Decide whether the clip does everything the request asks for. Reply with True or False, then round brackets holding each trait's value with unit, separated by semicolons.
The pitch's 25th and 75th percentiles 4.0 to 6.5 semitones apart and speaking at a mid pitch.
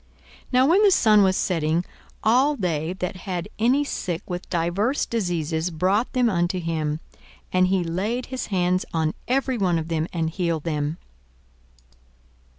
True (5.1 semitones; 180 Hz)